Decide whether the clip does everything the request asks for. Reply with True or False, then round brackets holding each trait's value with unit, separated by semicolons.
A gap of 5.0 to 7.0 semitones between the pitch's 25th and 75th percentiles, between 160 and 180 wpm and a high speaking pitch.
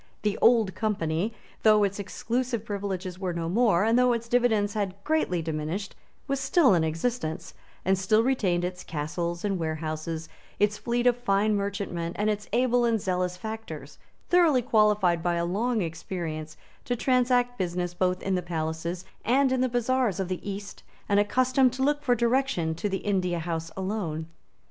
True (5.5 semitones; 170 wpm; 200 Hz)